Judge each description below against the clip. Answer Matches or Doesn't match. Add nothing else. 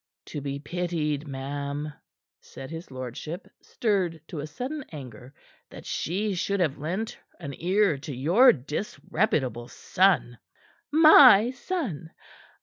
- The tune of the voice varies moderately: Doesn't match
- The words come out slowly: Matches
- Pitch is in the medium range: Matches